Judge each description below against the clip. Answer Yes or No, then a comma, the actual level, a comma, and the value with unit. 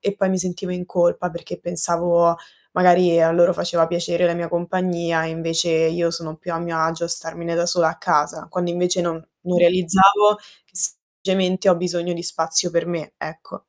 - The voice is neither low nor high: Yes, medium, 170 Hz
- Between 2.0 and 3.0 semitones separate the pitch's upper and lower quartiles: No, narrow, 1.3 semitones